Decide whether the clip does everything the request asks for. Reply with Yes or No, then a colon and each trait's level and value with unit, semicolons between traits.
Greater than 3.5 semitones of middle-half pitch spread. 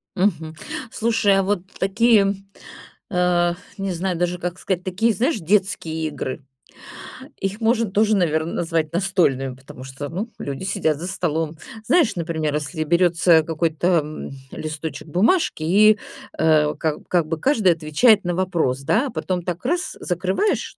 Yes: average, 3.9 semitones